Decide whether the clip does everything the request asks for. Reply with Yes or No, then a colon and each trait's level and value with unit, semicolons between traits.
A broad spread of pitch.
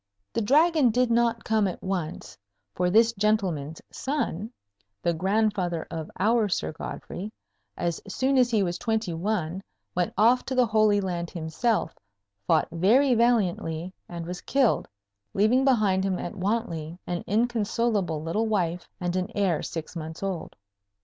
No: average, 4.9 semitones